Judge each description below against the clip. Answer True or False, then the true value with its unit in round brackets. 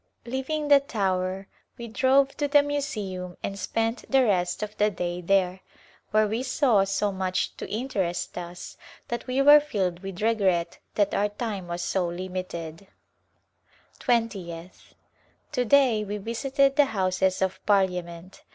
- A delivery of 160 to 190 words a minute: False (145 wpm)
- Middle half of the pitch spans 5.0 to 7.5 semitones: True (5.3 semitones)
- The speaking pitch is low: False (205 Hz)